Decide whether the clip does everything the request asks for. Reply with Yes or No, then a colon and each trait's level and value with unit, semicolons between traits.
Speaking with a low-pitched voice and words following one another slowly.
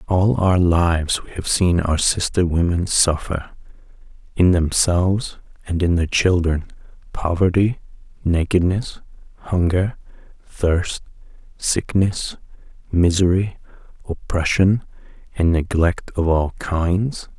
Yes: very low, 90 Hz; slow, 95 wpm